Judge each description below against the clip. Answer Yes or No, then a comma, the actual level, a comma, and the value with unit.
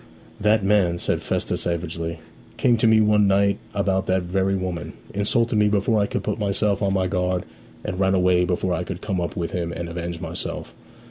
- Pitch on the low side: Yes, very low, 95 Hz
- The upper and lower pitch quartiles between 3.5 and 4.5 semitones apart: No, narrow, 2.6 semitones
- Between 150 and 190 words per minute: No, average, 200 wpm